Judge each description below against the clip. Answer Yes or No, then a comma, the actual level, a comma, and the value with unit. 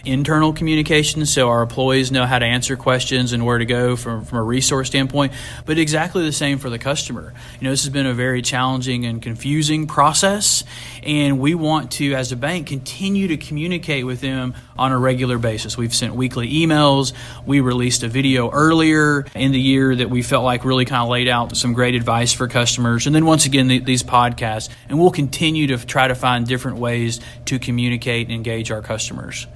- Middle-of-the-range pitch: No, low, 130 Hz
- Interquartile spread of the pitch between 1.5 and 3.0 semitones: Yes, average, 2.7 semitones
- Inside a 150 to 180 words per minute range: No, fast, 205 wpm